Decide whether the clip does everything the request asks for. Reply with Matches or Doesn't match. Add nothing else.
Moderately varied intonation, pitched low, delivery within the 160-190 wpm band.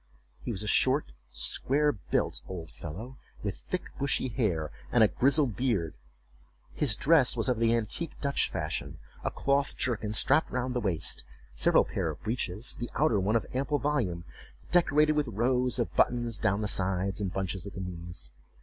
Doesn't match